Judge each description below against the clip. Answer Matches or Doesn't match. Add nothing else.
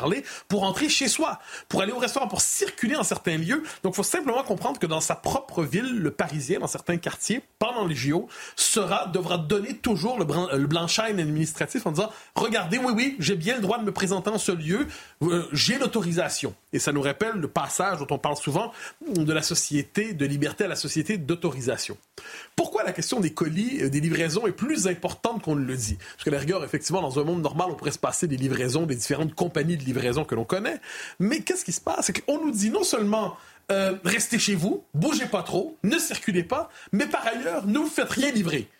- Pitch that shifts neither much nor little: Doesn't match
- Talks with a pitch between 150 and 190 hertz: Matches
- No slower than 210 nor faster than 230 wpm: Matches